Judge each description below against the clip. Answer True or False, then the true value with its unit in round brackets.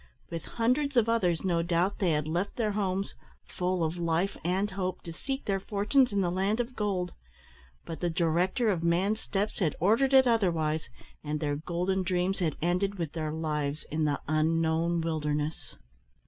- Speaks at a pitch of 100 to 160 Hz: False (180 Hz)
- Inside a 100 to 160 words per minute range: False (175 wpm)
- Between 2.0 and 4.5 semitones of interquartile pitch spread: True (3.8 semitones)